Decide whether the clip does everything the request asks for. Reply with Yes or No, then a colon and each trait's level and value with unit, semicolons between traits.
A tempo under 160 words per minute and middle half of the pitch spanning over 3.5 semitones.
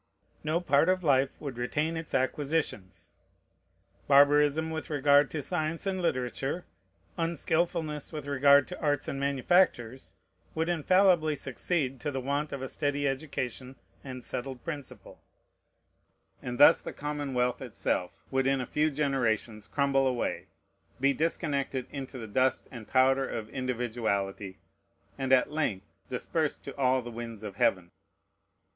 No: average, 140 wpm; average, 3.2 semitones